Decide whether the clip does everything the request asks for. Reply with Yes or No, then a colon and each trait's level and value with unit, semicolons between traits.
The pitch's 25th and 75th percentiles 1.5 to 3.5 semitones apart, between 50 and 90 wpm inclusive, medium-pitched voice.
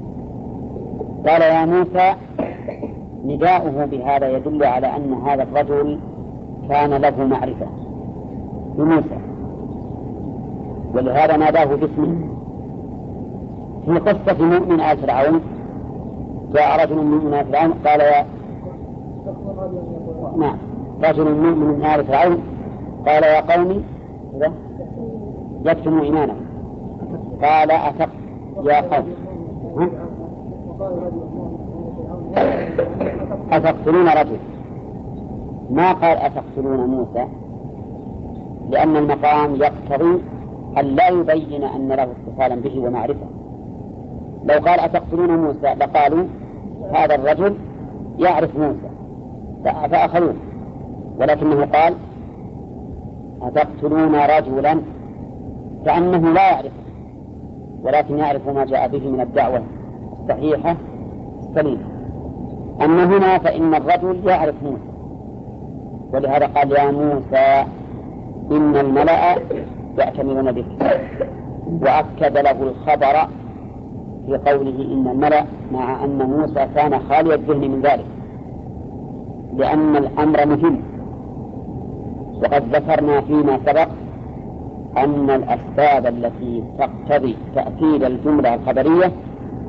Yes: narrow, 2.5 semitones; average, 85 wpm; medium, 145 Hz